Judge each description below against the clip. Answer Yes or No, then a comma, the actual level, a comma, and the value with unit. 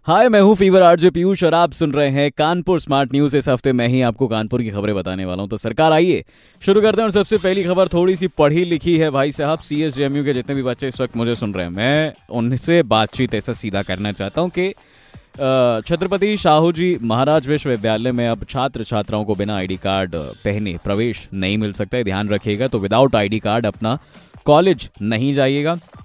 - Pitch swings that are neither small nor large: No, wide, 6.9 semitones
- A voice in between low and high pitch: No, low, 130 Hz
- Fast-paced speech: Yes, fast, 205 wpm